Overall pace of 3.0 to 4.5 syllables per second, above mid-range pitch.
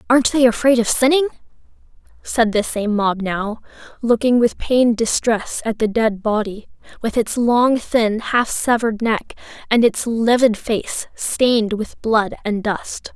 Yes: 4.2 syllables/s; high, 230 Hz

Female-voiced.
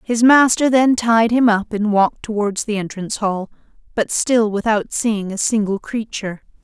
Yes: female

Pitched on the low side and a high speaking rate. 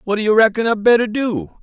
No: high, 210 Hz; fast, 220 wpm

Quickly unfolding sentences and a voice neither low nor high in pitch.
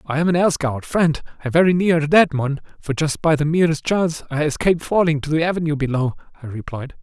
Yes: fast, 230 wpm; medium, 155 Hz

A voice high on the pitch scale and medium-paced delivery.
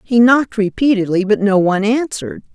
Yes: high, 215 Hz; average, 165 wpm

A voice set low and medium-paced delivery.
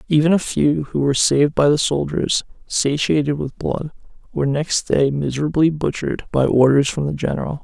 No: medium, 145 Hz; average, 175 wpm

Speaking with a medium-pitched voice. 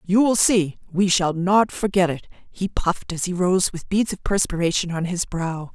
Yes: medium, 180 Hz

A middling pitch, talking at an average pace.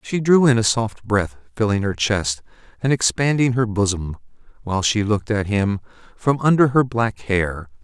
No: low, 110 Hz; average, 175 wpm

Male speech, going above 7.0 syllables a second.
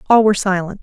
No: female; 7.9 syllables/s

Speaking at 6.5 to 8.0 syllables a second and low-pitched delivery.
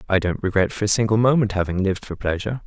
Yes: 7.3 syllables/s; low, 100 Hz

